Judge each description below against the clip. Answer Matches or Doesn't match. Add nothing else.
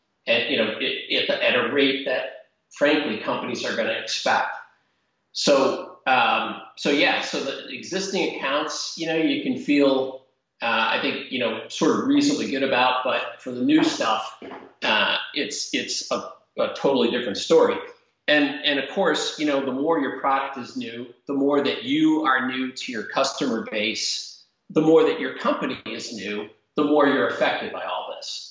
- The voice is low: Doesn't match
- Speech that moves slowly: Doesn't match